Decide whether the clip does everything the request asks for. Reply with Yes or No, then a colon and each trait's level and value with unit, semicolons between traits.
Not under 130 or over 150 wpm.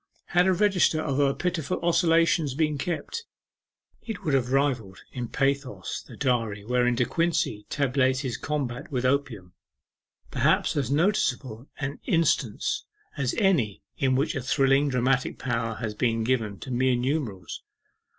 Yes: average, 145 wpm